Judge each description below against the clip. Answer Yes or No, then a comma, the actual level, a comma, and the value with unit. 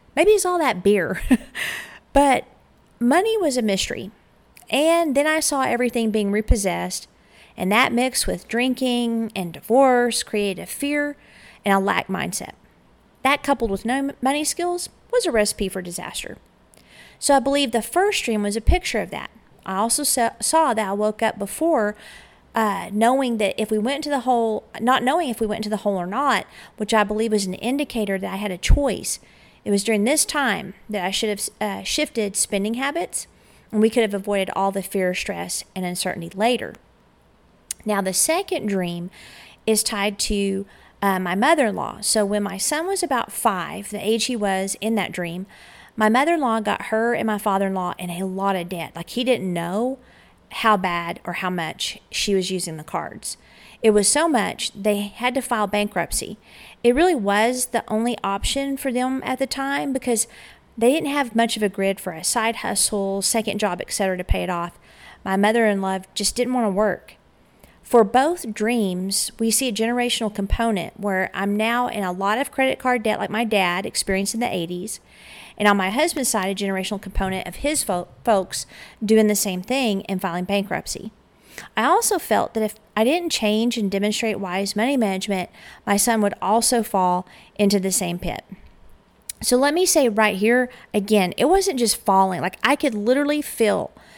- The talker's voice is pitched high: Yes, high, 215 Hz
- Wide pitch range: No, average, 4.3 semitones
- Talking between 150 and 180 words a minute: No, average, 190 wpm